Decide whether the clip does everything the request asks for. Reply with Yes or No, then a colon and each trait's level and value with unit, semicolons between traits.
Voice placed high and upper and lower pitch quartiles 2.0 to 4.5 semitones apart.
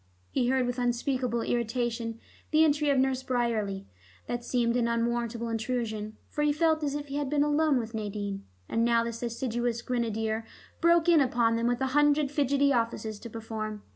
Yes: high, 240 Hz; average, 3.4 semitones